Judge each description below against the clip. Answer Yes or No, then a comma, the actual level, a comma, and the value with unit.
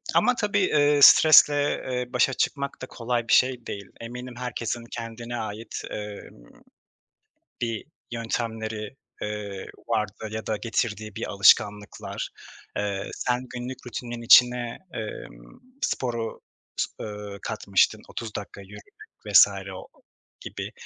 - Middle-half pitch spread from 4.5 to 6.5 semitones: No, average, 2.9 semitones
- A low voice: Yes, low, 115 Hz